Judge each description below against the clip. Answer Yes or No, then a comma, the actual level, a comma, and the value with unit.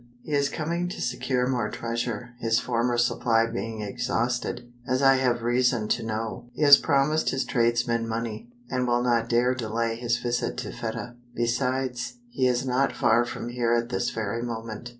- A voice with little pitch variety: Yes, narrow, 1.5 semitones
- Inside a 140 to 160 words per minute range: No, average, 175 wpm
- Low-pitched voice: Yes, low, 120 Hz